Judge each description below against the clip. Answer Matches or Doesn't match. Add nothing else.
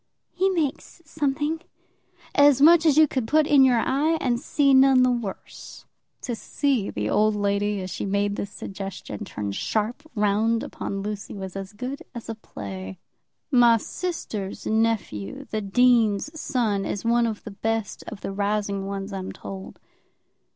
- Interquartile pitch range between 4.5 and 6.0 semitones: Matches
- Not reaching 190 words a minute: Matches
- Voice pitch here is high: Matches